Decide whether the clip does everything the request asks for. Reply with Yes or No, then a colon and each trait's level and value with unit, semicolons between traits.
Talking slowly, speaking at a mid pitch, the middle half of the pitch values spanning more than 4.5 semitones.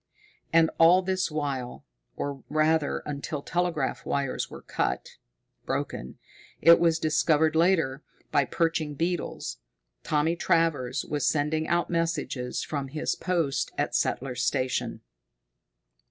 No: slow, 120 wpm; medium, 155 Hz; average, 3.0 semitones